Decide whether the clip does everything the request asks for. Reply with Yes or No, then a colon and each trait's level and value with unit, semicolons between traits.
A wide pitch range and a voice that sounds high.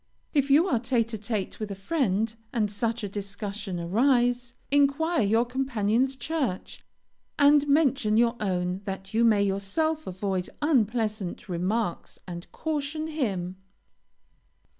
Yes: wide, 5.7 semitones; high, 225 Hz